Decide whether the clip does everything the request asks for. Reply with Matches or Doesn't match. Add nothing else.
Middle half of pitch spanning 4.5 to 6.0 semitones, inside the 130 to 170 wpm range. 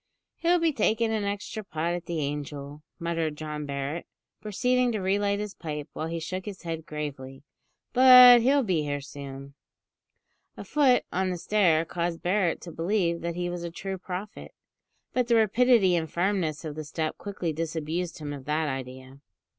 Doesn't match